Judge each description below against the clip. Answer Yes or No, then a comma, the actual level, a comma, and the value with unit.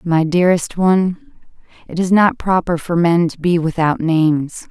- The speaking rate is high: No, average, 165 wpm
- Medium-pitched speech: Yes, medium, 170 Hz